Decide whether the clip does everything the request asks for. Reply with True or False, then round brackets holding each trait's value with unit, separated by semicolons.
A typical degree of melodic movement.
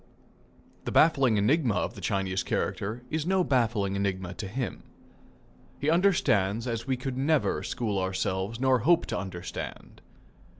False (5.7 semitones)